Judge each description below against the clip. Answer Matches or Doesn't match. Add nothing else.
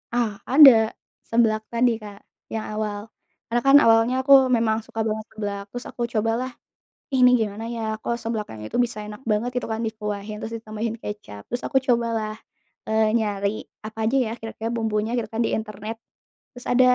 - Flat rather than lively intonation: Matches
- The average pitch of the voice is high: Matches